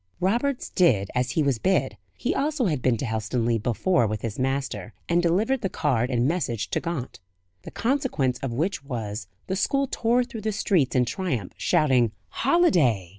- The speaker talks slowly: No, average, 175 wpm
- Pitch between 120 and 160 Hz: Yes, medium, 140 Hz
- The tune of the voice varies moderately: No, wide, 8.7 semitones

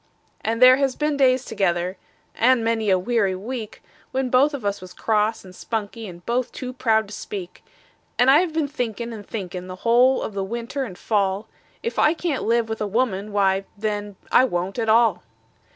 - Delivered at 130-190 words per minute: No, average, 200 wpm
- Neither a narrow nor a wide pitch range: Yes, average, 4.3 semitones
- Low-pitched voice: No, high, 225 Hz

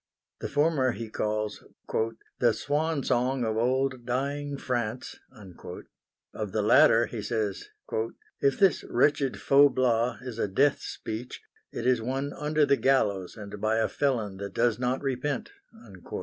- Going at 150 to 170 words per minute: No, average, 140 wpm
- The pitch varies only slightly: No, average, 3.8 semitones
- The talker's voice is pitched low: Yes, low, 125 Hz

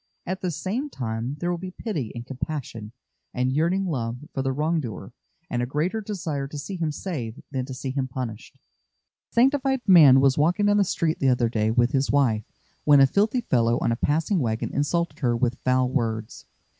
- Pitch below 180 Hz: Yes, medium, 140 Hz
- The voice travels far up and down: Yes, wide, 6.1 semitones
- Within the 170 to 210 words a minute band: Yes, fast, 205 wpm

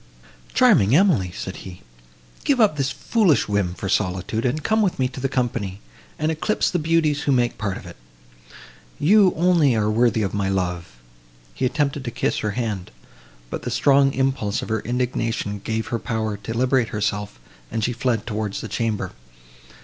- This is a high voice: No, low, 115 Hz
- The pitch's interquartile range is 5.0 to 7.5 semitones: Yes, average, 5.3 semitones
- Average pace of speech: Yes, average, 180 wpm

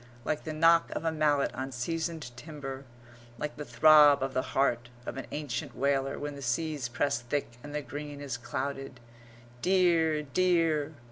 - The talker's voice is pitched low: No, medium, 145 Hz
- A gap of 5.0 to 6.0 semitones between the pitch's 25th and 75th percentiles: No, average, 2.7 semitones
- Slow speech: No, average, 165 wpm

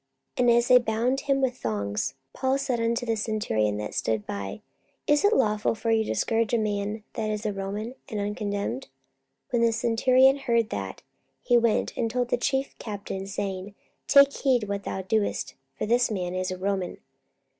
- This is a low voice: No, high, 220 Hz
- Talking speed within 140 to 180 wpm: No, average, 190 wpm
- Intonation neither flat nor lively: Yes, average, 3.4 semitones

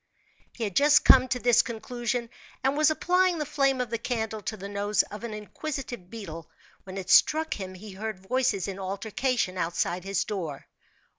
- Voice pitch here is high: Yes, high, 220 Hz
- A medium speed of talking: Yes, average, 180 wpm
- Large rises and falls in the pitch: No, average, 4.9 semitones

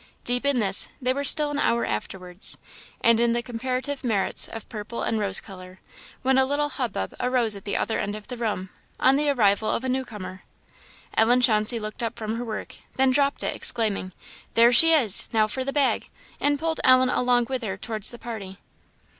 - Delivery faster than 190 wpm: Yes, fast, 205 wpm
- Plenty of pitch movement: No, average, 3.6 semitones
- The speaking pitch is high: Yes, high, 235 Hz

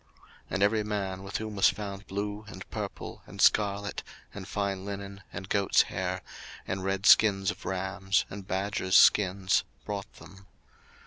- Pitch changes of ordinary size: No, narrow, 1.1 semitones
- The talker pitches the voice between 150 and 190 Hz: No, low, 100 Hz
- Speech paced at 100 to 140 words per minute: No, average, 155 wpm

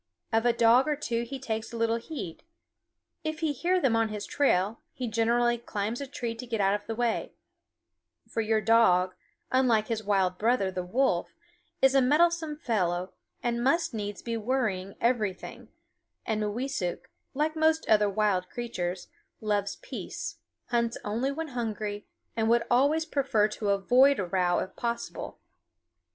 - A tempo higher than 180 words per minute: No, average, 160 wpm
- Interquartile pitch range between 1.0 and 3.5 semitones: No, average, 3.9 semitones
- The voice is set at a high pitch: Yes, high, 230 Hz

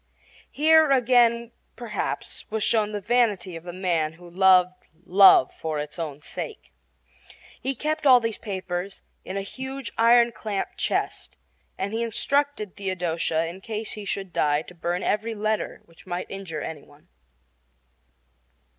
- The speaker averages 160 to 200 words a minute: No, average, 145 wpm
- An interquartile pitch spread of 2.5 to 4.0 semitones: No, average, 4.9 semitones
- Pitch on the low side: No, high, 200 Hz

